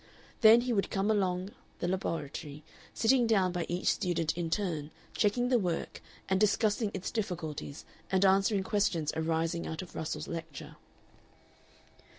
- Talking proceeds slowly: No, average, 145 wpm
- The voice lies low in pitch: No, medium, 185 Hz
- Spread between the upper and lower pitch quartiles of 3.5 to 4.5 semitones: Yes, average, 4.0 semitones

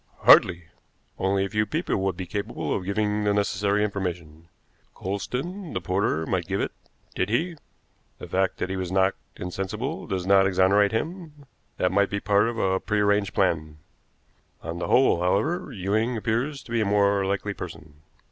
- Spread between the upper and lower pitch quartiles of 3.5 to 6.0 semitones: No, narrow, 2.5 semitones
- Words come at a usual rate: Yes, average, 170 wpm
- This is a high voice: No, low, 100 Hz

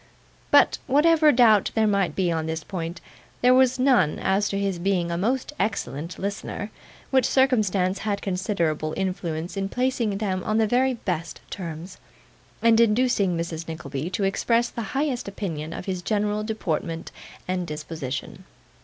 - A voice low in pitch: No, high, 195 Hz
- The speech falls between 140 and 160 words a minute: Yes, average, 155 wpm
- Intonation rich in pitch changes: No, average, 5.0 semitones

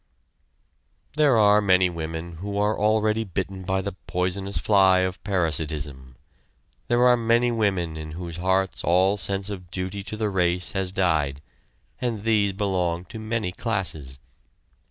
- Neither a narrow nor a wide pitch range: Yes, average, 3.1 semitones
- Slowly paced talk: No, average, 145 wpm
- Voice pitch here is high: No, very low, 95 Hz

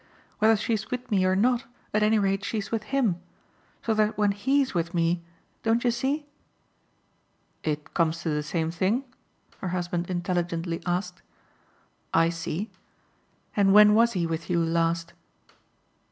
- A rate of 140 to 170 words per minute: Yes, average, 155 wpm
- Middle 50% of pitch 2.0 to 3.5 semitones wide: No, average, 4.4 semitones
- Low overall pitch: No, medium, 185 Hz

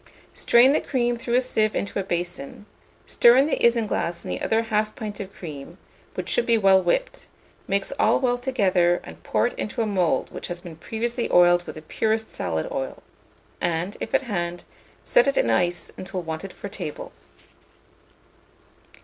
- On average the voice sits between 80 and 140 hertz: No, high, 200 Hz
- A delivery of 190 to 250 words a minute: No, average, 180 wpm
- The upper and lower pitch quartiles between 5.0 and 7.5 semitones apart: Yes, average, 5.3 semitones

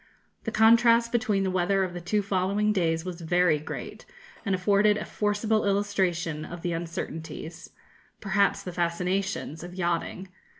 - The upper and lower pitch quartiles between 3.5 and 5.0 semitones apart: No, average, 3.0 semitones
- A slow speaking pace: No, average, 145 wpm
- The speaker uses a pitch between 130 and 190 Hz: Yes, medium, 185 Hz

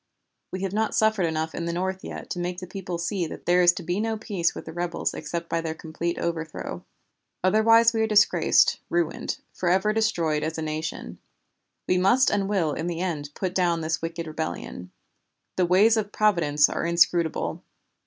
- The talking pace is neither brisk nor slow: Yes, average, 190 wpm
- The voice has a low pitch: No, medium, 175 Hz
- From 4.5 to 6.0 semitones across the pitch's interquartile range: No, average, 3.2 semitones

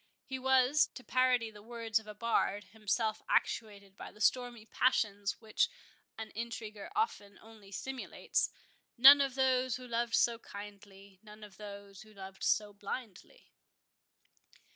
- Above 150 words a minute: No, average, 140 wpm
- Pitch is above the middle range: Yes, high, 220 Hz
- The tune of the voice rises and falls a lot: No, average, 3.6 semitones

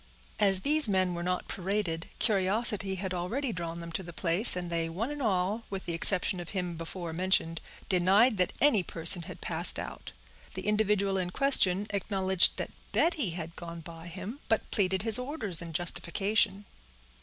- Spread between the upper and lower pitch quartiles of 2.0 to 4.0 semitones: Yes, average, 3.4 semitones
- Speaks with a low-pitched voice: No, medium, 185 Hz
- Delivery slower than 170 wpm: No, average, 175 wpm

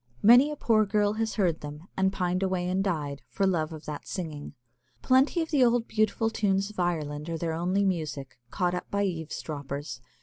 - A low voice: No, medium, 185 Hz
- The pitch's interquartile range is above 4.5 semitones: Yes, average, 5.1 semitones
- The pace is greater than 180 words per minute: Yes, average, 195 wpm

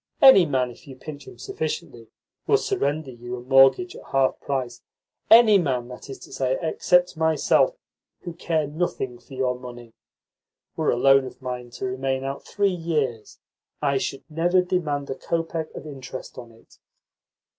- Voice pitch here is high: No, low, 135 Hz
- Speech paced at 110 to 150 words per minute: No, average, 165 wpm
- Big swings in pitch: No, average, 4.3 semitones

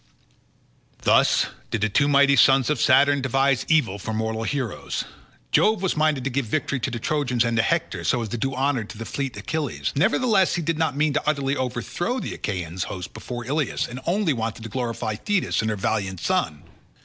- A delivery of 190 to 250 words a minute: Yes, average, 195 wpm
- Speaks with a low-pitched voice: Yes, low, 130 Hz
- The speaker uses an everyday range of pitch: Yes, average, 4.8 semitones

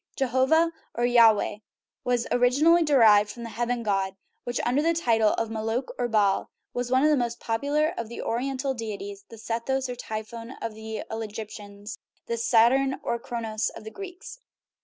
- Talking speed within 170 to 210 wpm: Yes, average, 175 wpm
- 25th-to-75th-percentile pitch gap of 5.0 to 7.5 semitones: No, average, 3.2 semitones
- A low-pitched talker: No, high, 235 Hz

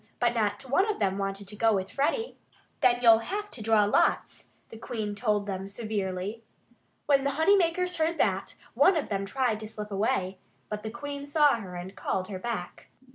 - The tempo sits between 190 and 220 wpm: Yes, average, 195 wpm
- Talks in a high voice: Yes, high, 220 Hz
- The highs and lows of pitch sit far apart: Yes, wide, 6.0 semitones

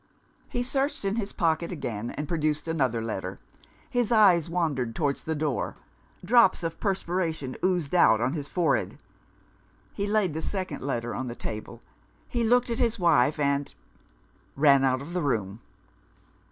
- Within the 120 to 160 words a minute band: Yes, average, 155 wpm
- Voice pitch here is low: No, medium, 160 Hz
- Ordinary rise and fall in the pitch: No, wide, 6.3 semitones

